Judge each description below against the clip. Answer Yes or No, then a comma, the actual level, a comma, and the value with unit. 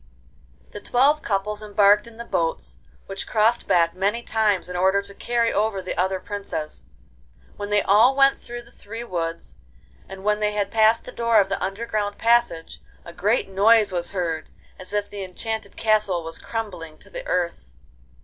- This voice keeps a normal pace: Yes, average, 180 wpm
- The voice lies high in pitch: Yes, high, 205 Hz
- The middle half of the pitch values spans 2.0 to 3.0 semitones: No, average, 3.4 semitones